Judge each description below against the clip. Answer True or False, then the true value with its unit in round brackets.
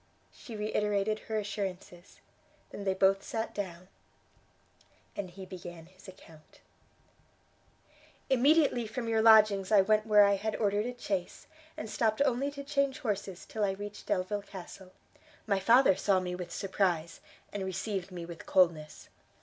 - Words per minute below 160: True (150 wpm)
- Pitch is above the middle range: True (200 Hz)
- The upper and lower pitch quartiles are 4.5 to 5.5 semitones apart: False (2.8 semitones)